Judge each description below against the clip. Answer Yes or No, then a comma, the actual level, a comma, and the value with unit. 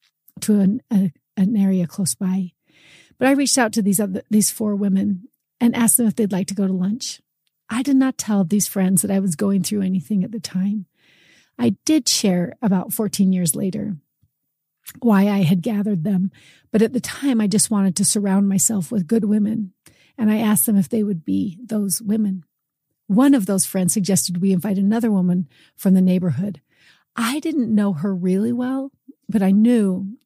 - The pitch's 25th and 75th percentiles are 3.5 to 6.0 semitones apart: No, average, 2.9 semitones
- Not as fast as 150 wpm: No, average, 195 wpm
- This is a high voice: Yes, high, 200 Hz